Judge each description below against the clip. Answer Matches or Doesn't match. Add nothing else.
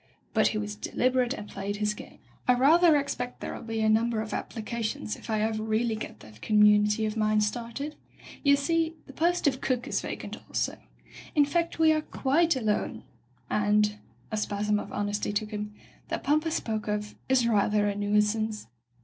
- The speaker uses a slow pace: Doesn't match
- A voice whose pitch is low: Doesn't match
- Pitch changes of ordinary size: Matches